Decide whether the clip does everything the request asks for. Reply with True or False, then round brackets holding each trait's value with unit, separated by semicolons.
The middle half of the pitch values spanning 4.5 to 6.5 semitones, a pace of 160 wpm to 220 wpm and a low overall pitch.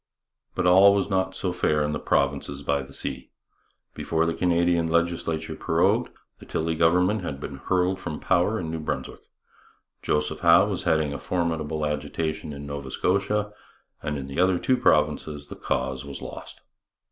False (3.5 semitones; 170 wpm; 80 Hz)